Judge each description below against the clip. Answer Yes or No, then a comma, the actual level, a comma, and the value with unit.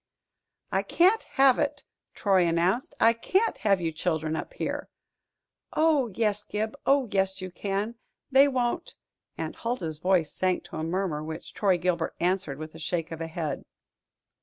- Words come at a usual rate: Yes, average, 165 wpm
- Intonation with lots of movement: Yes, wide, 6.0 semitones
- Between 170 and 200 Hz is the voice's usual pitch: Yes, high, 190 Hz